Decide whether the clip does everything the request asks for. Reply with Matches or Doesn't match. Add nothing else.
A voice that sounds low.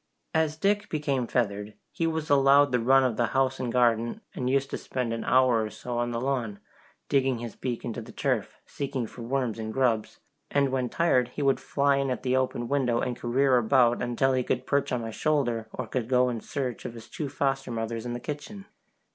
Matches